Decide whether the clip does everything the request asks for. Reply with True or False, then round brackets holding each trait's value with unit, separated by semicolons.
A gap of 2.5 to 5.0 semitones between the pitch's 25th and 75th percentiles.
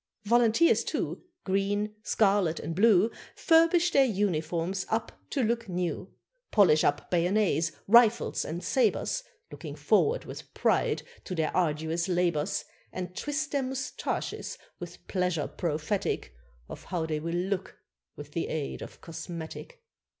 False (5.5 semitones)